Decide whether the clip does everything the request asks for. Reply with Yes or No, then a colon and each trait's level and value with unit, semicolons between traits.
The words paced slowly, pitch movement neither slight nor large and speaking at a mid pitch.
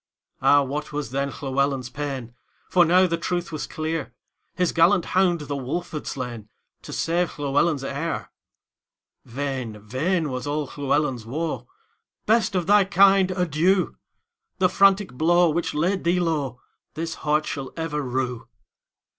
Yes: slow, 120 wpm; average, 4.5 semitones; medium, 155 Hz